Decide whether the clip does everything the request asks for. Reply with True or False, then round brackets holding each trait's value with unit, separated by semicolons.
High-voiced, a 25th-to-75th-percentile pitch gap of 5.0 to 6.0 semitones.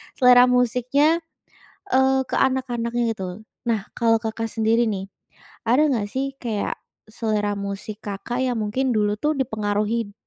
False (230 Hz; 3.3 semitones)